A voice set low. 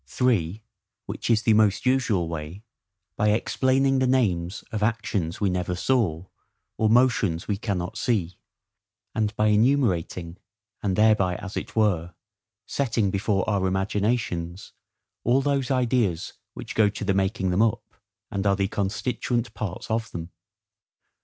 Yes: low, 105 Hz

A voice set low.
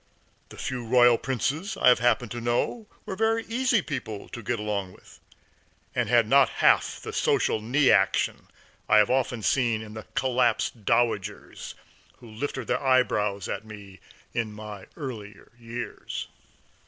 Yes: low, 120 Hz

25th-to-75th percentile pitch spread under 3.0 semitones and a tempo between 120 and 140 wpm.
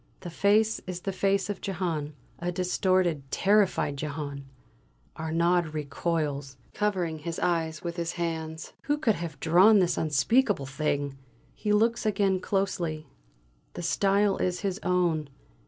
No: average, 3.8 semitones; slow, 135 wpm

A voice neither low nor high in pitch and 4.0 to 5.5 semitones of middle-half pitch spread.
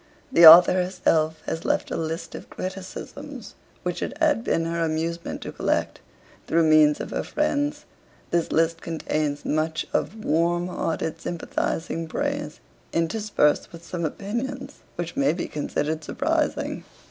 No: medium, 165 Hz; average, 2.9 semitones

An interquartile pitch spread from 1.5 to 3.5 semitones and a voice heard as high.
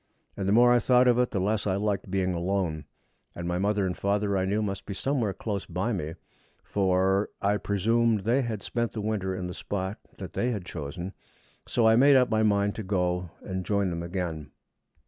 No: average, 2.9 semitones; low, 100 Hz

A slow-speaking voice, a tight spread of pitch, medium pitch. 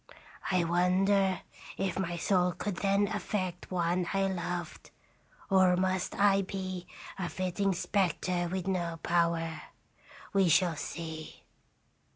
Yes: slow, 120 wpm; narrow, 1.9 semitones; medium, 180 Hz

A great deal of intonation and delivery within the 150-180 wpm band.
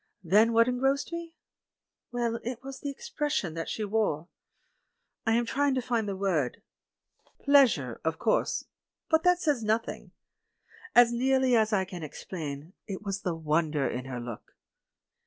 Yes: wide, 7.8 semitones; average, 170 wpm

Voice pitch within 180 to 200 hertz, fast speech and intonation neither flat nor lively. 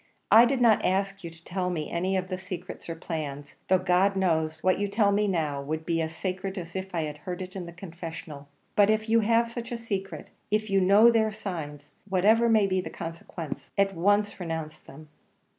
Yes: medium, 185 Hz; fast, 210 wpm; average, 3.7 semitones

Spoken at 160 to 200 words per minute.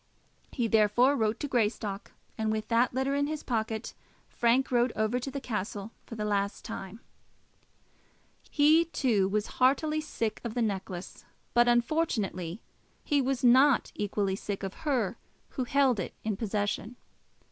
No: average, 150 wpm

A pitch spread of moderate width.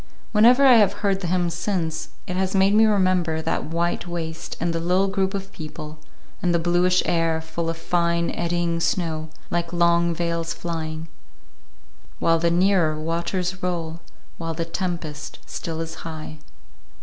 No: narrow, 1.8 semitones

